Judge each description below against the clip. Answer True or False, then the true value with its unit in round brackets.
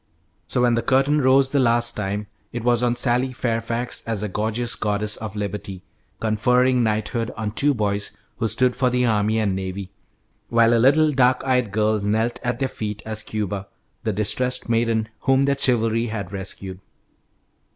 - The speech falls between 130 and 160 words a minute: False (170 wpm)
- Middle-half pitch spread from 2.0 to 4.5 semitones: True (2.9 semitones)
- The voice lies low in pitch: True (115 Hz)